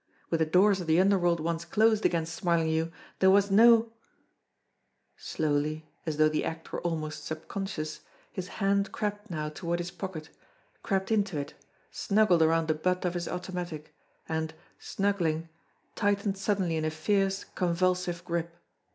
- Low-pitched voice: No, medium, 175 Hz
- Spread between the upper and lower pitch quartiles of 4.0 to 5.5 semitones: No, average, 3.5 semitones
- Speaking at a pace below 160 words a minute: Yes, average, 150 wpm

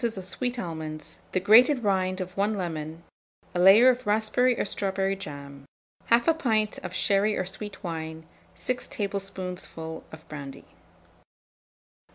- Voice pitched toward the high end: Yes, high, 195 Hz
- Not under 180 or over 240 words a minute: No, slow, 135 wpm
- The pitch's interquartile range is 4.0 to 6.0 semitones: Yes, average, 4.8 semitones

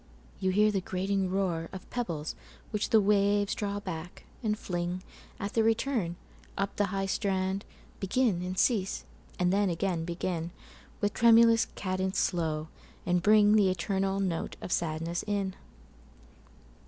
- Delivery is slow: Yes, slow, 125 wpm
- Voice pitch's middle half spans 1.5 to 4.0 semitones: Yes, narrow, 2.5 semitones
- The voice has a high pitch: Yes, high, 195 Hz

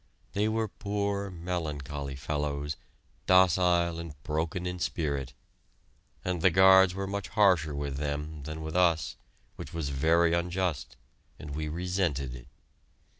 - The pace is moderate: No, slow, 130 wpm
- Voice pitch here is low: Yes, very low, 85 Hz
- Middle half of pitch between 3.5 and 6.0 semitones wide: Yes, average, 3.8 semitones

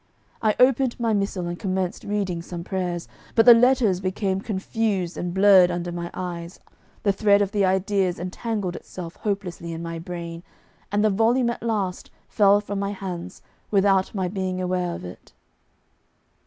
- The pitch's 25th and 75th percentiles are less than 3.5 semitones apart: Yes, narrow, 2.6 semitones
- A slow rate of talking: No, average, 165 wpm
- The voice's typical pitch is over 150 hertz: Yes, high, 190 Hz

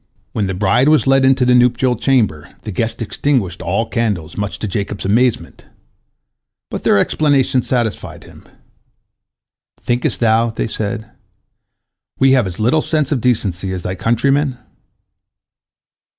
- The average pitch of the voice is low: Yes, low, 115 Hz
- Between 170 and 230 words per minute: No, average, 140 wpm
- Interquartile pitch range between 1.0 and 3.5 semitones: No, average, 4.4 semitones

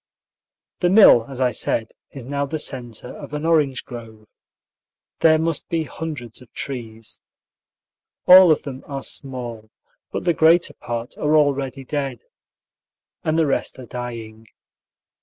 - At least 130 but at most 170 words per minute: Yes, average, 140 wpm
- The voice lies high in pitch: No, low, 135 Hz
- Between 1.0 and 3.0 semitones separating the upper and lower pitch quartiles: No, average, 4.4 semitones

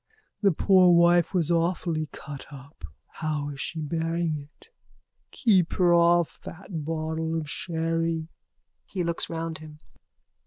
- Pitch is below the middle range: No, medium, 165 Hz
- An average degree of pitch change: No, narrow, 1.7 semitones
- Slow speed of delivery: Yes, slow, 130 wpm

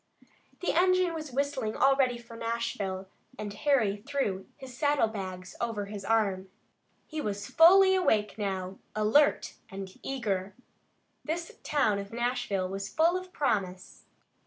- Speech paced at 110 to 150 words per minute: Yes, slow, 135 wpm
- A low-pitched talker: No, high, 230 Hz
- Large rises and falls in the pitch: Yes, wide, 6.3 semitones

